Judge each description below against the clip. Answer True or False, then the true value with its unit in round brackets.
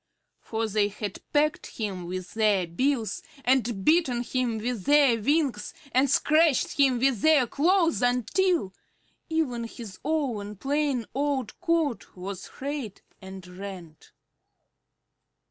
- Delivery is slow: True (120 wpm)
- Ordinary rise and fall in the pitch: False (6.0 semitones)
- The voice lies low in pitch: False (245 Hz)